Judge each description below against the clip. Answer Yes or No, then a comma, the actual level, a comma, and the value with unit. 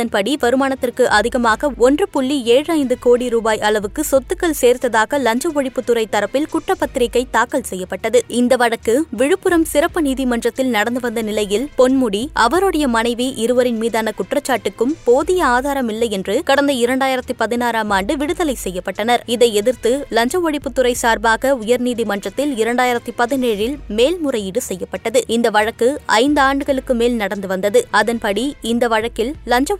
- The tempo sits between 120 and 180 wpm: Yes, average, 125 wpm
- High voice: Yes, high, 245 Hz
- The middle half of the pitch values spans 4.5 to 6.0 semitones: No, average, 3.4 semitones